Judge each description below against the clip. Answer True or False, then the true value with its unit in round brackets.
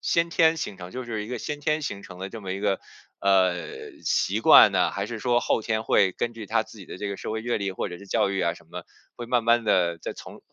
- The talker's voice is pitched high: False (105 Hz)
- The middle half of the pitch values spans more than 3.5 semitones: True (3.9 semitones)